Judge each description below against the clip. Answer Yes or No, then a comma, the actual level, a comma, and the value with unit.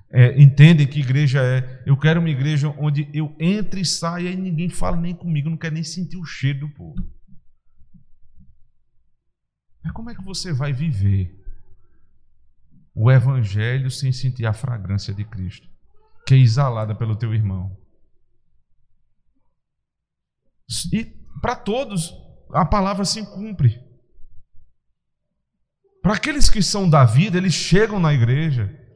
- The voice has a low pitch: No, medium, 145 Hz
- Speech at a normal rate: Yes, average, 135 wpm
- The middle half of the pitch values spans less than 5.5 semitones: No, wide, 6.9 semitones